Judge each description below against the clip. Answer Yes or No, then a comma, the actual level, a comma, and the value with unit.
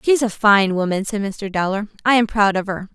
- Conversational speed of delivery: No, fast, 245 wpm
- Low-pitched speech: No, high, 205 Hz